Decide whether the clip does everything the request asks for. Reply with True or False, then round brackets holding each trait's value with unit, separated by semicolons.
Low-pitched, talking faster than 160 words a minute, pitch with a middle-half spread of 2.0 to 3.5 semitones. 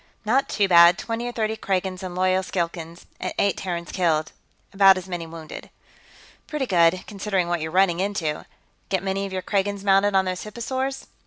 False (190 Hz; 180 wpm; 2.7 semitones)